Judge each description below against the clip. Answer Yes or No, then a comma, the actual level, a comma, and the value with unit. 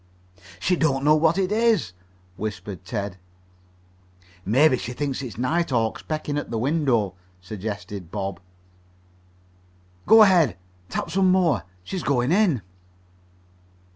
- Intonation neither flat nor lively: No, wide, 8.0 semitones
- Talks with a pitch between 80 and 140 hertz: Yes, low, 135 Hz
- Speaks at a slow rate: Yes, slow, 120 wpm